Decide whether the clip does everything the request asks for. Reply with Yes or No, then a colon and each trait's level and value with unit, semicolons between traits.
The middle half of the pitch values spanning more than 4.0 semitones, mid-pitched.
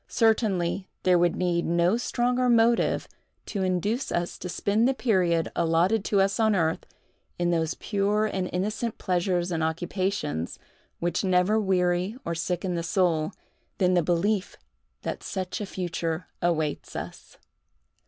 No: average, 3.3 semitones; medium, 180 Hz